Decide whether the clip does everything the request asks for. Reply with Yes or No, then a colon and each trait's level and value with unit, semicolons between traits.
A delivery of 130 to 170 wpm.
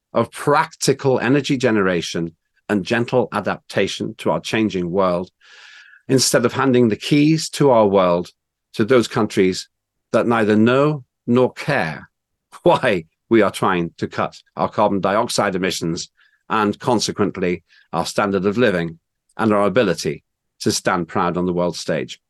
Yes: average, 145 wpm